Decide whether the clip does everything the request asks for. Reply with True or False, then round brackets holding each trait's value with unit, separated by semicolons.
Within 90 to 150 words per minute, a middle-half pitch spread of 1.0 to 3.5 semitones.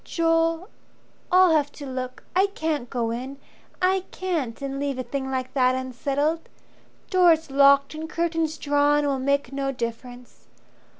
False (145 wpm; 4.0 semitones)